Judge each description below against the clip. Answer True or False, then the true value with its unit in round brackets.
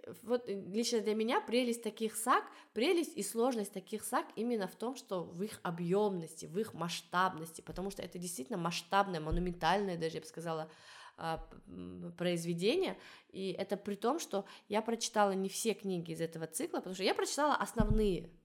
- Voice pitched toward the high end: True (195 Hz)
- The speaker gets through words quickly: True (165 wpm)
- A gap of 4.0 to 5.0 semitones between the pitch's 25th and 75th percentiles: True (4.4 semitones)